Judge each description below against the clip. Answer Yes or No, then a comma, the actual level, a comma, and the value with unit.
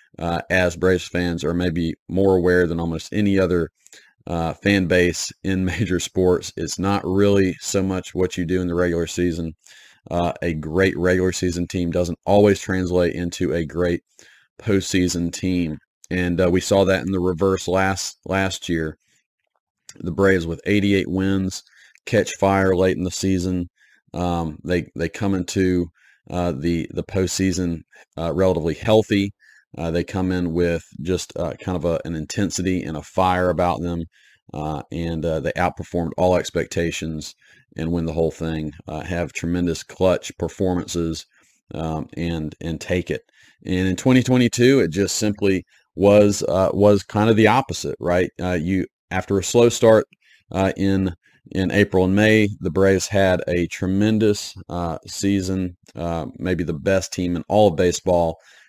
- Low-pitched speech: Yes, very low, 90 Hz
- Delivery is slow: No, average, 165 wpm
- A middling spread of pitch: No, narrow, 2.1 semitones